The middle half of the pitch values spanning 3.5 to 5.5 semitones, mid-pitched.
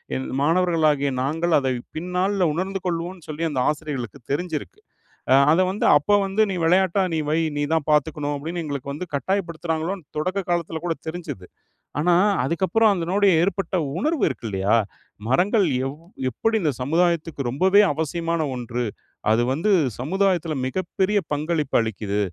Yes: average, 4.2 semitones; medium, 165 Hz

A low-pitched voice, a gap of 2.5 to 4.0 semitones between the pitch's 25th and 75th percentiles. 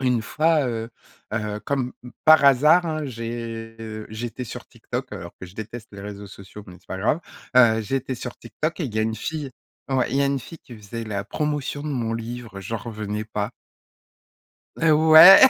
No: low, 115 Hz; average, 4.5 semitones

